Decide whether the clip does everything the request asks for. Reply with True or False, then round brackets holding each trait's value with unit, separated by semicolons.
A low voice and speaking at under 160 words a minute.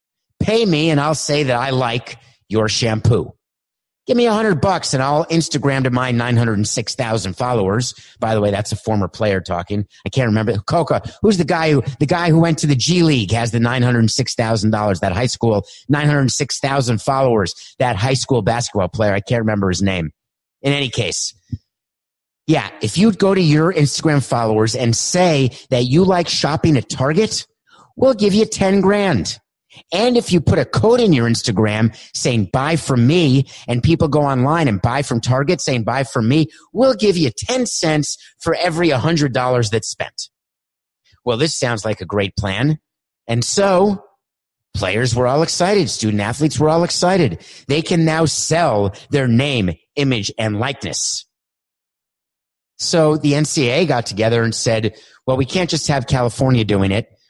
False (130 Hz; 175 wpm)